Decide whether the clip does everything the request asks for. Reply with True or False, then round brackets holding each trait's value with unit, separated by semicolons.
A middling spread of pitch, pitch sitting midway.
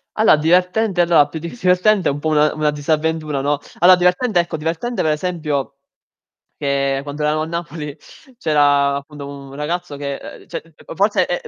True (3.4 semitones; 155 Hz)